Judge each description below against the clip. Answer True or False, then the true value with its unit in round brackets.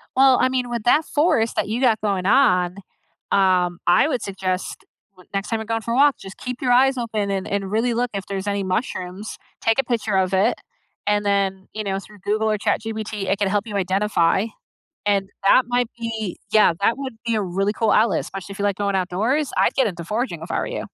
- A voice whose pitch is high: True (210 Hz)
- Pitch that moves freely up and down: False (3.4 semitones)